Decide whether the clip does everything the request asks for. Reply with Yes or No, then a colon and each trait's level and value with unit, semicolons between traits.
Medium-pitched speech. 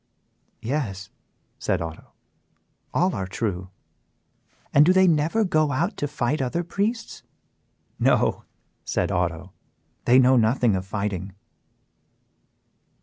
No: low, 130 Hz